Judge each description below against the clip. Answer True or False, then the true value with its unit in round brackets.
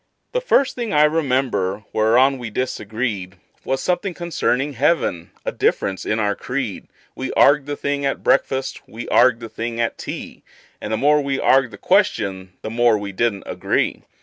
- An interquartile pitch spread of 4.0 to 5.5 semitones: True (4.7 semitones)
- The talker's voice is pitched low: True (125 Hz)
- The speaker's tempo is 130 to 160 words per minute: False (175 wpm)